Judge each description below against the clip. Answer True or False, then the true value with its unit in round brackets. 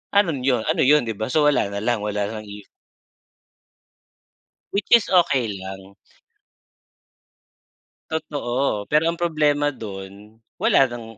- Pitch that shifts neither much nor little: False (6.3 semitones)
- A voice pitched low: True (120 Hz)